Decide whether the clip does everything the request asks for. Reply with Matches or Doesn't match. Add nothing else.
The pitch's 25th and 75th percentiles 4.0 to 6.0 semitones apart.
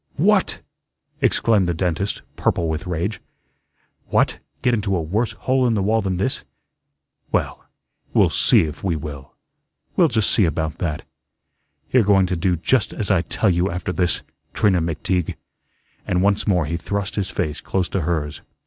Doesn't match